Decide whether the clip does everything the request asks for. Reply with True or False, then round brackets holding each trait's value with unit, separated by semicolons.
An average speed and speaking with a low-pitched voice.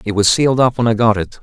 False (335 wpm; 110 Hz)